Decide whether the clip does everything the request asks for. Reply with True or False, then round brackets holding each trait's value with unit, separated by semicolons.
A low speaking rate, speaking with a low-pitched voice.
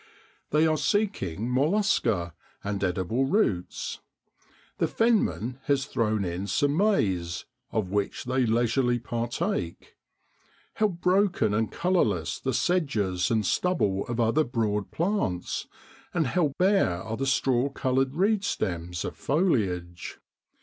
True (120 wpm; 120 Hz)